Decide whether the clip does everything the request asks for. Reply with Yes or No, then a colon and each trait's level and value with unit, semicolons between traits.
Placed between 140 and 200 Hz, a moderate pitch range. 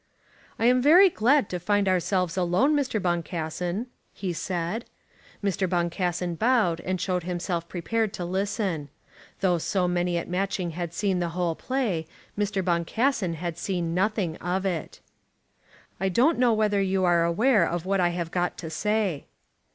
Yes: medium, 185 Hz; average, 3.3 semitones